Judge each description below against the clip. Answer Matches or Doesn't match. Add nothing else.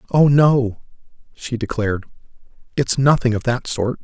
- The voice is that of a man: Matches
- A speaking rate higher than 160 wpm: Doesn't match